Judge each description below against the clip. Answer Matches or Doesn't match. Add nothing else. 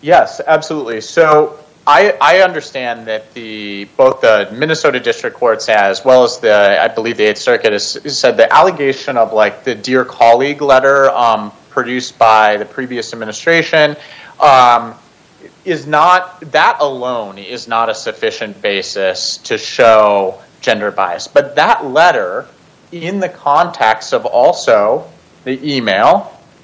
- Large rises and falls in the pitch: Matches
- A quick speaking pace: Doesn't match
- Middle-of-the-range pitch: Doesn't match